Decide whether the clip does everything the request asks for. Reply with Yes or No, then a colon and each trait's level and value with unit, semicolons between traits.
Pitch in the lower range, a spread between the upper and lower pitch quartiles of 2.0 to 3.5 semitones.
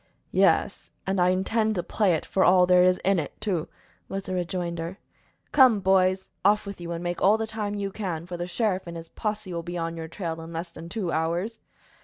No: medium, 185 Hz; average, 2.9 semitones